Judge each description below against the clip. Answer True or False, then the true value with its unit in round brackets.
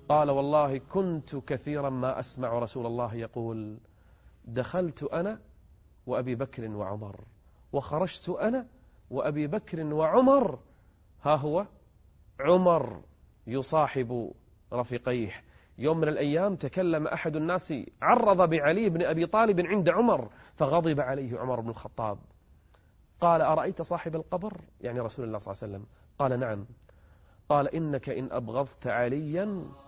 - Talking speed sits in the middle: True (120 wpm)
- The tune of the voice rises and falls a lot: True (6.8 semitones)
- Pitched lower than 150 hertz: True (135 Hz)